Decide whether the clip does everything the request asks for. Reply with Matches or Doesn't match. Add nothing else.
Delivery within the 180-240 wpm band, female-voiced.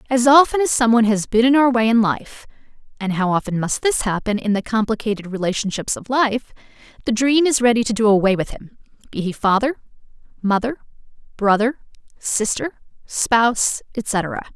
Doesn't match